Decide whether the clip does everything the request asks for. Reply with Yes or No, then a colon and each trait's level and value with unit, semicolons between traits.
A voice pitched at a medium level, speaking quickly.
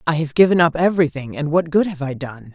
Yes: medium, 160 Hz; fast, 235 wpm